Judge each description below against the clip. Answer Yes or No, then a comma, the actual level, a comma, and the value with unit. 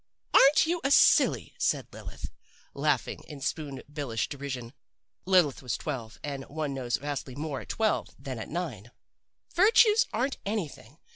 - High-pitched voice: No, medium, 145 Hz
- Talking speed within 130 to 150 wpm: Yes, average, 145 wpm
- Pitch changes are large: Yes, wide, 6.8 semitones